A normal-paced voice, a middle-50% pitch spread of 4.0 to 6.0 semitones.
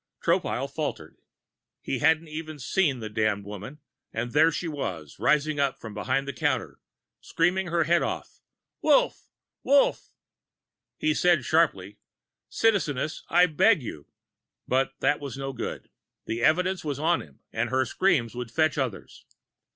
Yes: average, 150 wpm; wide, 5.5 semitones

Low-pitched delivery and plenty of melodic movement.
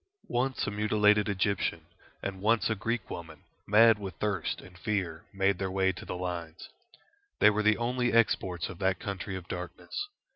No: low, 100 Hz; average, 2.8 semitones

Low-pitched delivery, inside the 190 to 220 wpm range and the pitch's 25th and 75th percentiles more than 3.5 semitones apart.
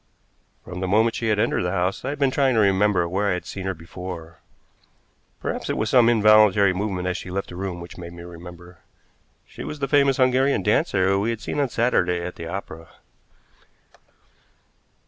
Yes: very low, 95 Hz; average, 195 wpm; average, 4.1 semitones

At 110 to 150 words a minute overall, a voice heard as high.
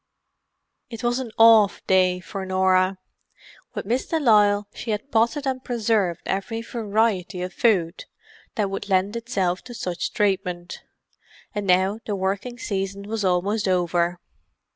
Yes: average, 140 wpm; high, 200 Hz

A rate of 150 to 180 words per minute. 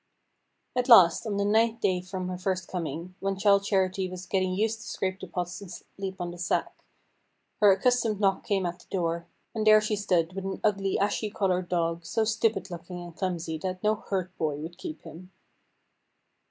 No: average, 195 wpm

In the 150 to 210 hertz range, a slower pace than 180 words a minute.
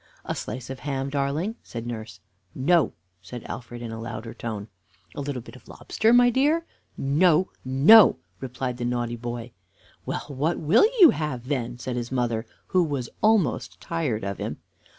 No: low, 130 Hz; average, 170 wpm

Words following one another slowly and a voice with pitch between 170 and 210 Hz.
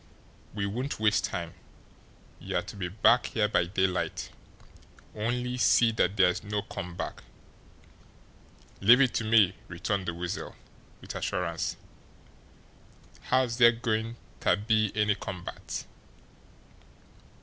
No: slow, 120 wpm; low, 105 Hz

